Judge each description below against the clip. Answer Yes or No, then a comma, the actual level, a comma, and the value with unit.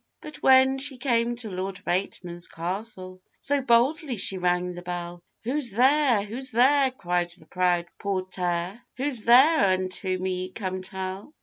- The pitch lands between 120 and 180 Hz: No, high, 195 Hz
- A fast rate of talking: No, average, 145 wpm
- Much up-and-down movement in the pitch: Yes, wide, 5.8 semitones